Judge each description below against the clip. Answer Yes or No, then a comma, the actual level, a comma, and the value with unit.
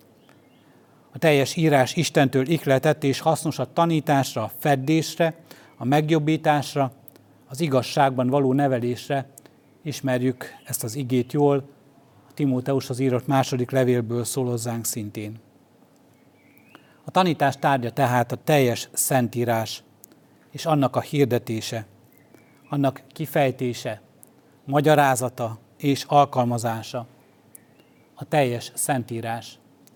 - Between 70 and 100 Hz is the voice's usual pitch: No, low, 135 Hz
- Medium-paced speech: No, slow, 100 wpm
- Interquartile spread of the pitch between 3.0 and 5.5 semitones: Yes, average, 3.4 semitones